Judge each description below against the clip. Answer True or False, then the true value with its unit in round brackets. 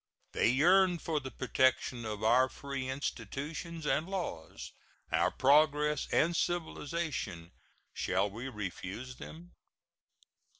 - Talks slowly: True (110 wpm)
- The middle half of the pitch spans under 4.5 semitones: False (5.2 semitones)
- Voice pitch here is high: False (140 Hz)